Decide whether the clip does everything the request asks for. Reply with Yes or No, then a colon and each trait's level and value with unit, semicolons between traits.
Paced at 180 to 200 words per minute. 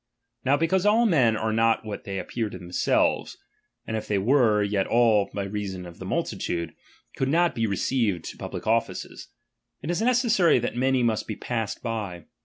Yes: average, 190 wpm